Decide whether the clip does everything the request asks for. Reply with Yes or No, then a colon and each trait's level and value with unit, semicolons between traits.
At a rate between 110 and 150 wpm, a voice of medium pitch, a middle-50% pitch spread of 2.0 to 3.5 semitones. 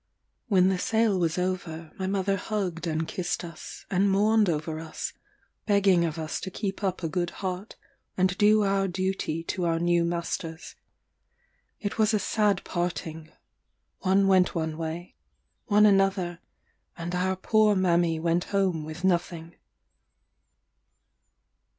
Yes: average, 140 wpm; medium, 180 Hz; average, 2.7 semitones